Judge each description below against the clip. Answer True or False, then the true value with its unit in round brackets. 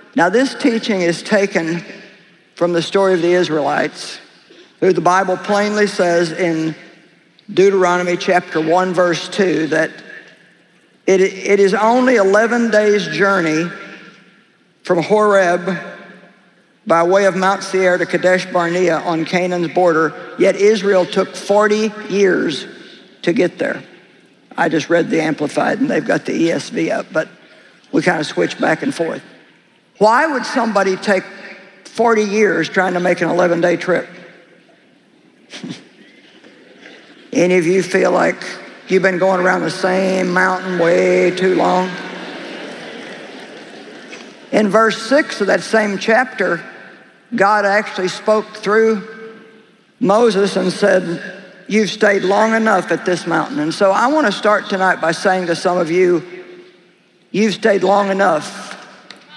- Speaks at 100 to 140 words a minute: True (135 wpm)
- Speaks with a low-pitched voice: False (190 Hz)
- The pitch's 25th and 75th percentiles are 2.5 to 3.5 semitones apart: True (2.8 semitones)